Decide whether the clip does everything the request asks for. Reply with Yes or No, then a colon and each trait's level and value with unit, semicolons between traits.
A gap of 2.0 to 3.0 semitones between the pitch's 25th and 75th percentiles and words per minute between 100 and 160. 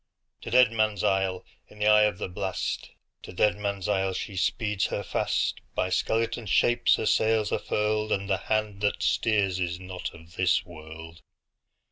Yes: average, 2.7 semitones; average, 150 wpm